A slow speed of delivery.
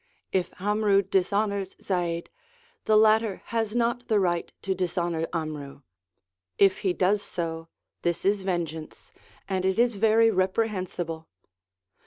Yes: slow, 125 wpm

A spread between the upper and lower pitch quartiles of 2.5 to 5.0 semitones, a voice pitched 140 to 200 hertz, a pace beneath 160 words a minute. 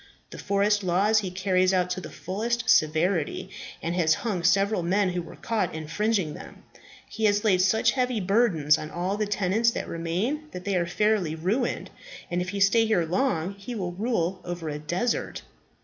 No: average, 3.6 semitones; high, 190 Hz; average, 185 wpm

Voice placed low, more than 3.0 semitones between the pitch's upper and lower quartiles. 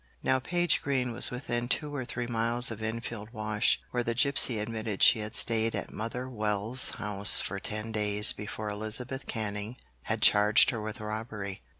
No: low, 110 Hz; narrow, 2.5 semitones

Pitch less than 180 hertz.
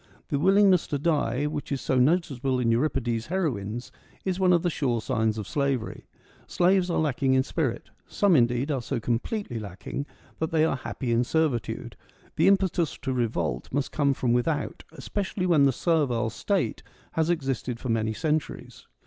Yes: medium, 140 Hz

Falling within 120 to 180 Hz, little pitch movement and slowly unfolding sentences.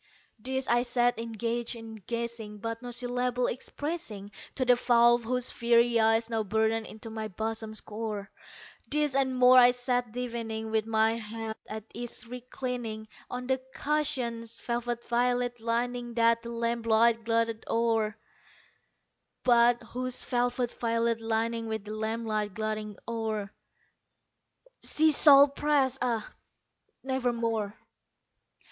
No: high, 235 Hz; narrow, 1.8 semitones; slow, 130 wpm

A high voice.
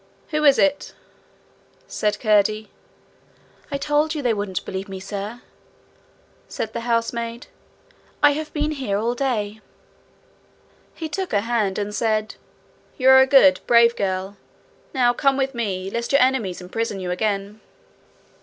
Yes: high, 230 Hz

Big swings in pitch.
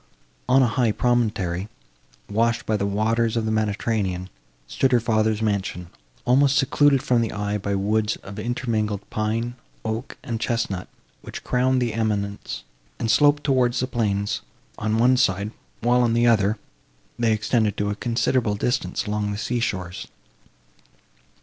No: average, 2.8 semitones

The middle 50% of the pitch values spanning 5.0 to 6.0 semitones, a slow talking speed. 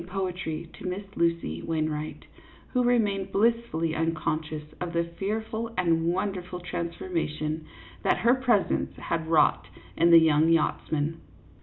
No: average, 3.4 semitones; slow, 130 wpm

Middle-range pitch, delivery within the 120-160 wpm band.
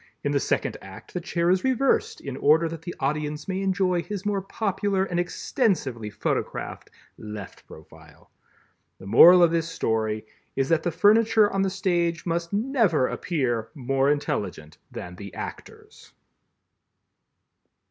Yes: medium, 170 Hz; average, 145 wpm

